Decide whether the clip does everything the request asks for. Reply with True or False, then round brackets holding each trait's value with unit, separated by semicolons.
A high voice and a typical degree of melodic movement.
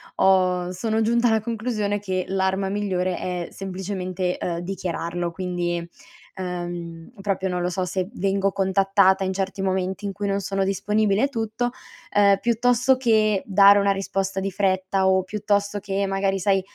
False (195 Hz; 1.7 semitones)